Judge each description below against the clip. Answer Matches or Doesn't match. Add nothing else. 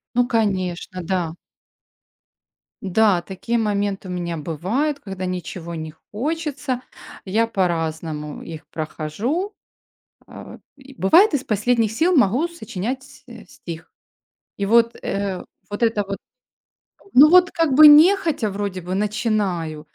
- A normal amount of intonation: Doesn't match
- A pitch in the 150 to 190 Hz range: Doesn't match